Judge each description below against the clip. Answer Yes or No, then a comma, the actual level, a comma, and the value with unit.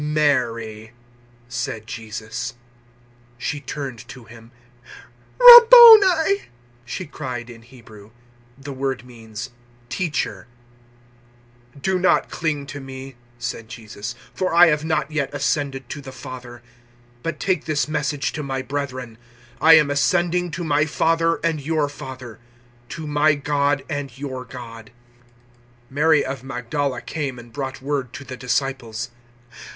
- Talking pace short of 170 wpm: Yes, slow, 135 wpm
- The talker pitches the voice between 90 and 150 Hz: Yes, low, 135 Hz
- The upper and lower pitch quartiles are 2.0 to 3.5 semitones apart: No, average, 3.9 semitones